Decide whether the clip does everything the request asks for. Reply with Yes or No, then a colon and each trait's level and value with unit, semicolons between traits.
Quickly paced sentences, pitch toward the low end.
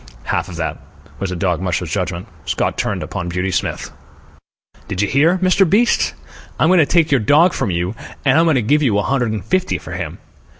Yes: fast, 215 wpm; low, 125 Hz